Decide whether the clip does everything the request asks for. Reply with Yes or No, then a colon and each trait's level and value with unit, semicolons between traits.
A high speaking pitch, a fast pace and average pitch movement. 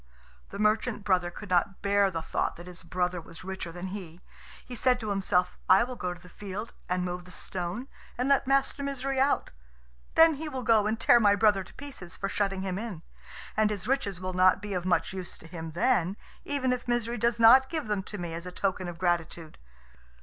Yes: high, 195 Hz; fast, 220 wpm; average, 4.8 semitones